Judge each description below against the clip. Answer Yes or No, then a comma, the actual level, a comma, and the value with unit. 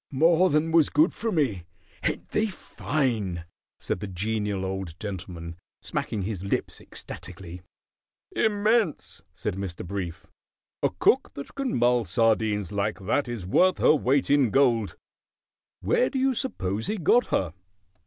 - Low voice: Yes, low, 110 Hz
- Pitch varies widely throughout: Yes, wide, 8.4 semitones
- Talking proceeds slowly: No, average, 145 wpm